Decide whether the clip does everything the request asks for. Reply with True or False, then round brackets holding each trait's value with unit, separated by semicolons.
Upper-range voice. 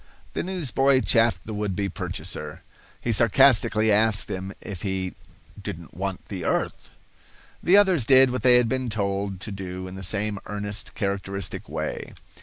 False (105 Hz)